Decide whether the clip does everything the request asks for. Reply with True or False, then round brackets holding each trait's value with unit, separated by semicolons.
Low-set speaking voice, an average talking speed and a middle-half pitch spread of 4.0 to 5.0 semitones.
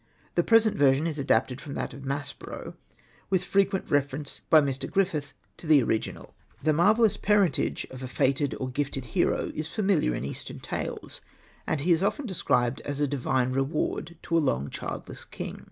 False (145 Hz; 175 wpm; 4.6 semitones)